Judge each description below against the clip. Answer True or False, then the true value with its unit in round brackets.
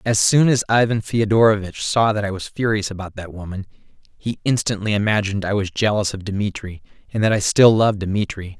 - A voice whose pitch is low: True (105 Hz)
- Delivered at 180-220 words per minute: True (190 wpm)